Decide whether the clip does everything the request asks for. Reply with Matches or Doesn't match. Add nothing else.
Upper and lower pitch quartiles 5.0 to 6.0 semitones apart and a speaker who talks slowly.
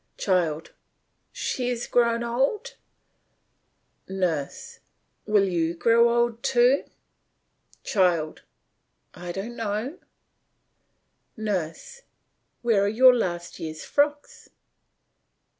Matches